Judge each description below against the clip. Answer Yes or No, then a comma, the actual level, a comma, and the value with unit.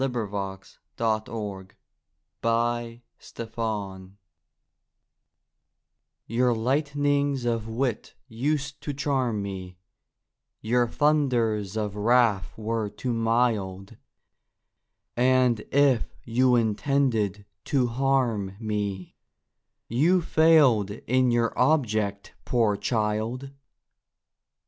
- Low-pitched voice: Yes, low, 115 Hz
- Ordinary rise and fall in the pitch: Yes, average, 3.6 semitones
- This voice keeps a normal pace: No, slow, 85 wpm